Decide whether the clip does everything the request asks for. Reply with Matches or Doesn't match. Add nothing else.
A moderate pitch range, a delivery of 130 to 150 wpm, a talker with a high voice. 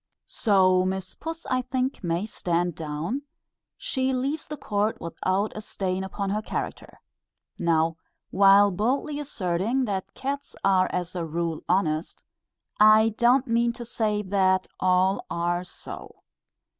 Matches